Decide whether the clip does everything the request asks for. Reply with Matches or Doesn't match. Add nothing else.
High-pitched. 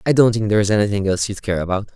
Doesn't match